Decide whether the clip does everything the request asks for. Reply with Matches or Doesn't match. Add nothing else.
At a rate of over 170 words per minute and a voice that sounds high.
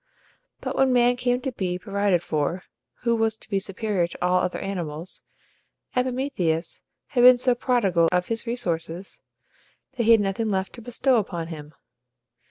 Doesn't match